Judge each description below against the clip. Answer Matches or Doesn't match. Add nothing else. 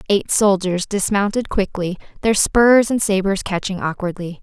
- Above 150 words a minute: Doesn't match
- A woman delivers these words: Matches